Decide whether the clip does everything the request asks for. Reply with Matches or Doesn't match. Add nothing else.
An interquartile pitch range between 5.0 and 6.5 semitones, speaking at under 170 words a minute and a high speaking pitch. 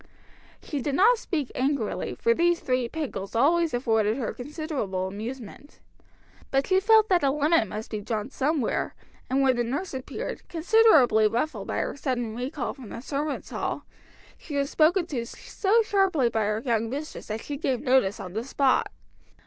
Doesn't match